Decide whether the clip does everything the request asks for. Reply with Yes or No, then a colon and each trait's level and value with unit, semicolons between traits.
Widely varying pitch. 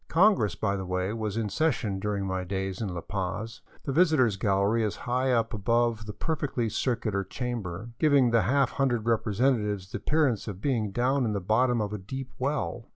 No: average, 4.3 semitones